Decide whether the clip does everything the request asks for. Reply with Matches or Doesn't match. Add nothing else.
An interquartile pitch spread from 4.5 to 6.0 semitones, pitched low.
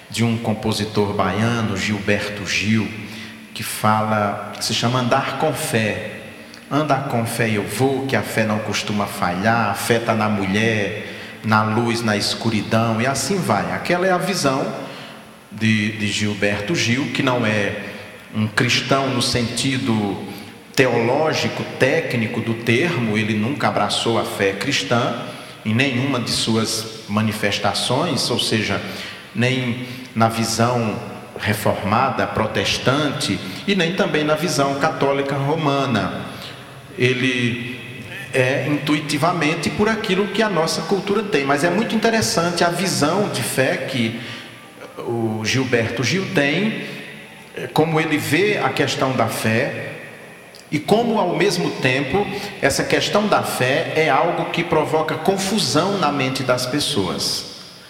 Matches